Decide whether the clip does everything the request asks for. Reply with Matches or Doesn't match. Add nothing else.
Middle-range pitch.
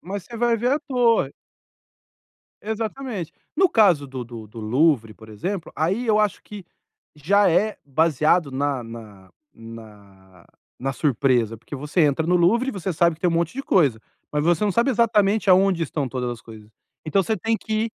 Matches